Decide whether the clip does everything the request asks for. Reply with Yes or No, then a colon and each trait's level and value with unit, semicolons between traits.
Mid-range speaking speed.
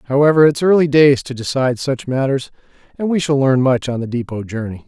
No: fast, 210 wpm